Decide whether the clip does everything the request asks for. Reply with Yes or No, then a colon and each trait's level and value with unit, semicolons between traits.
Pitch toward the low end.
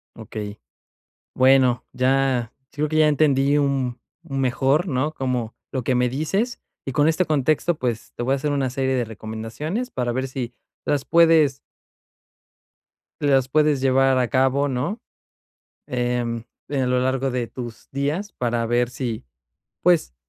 Yes: low, 130 Hz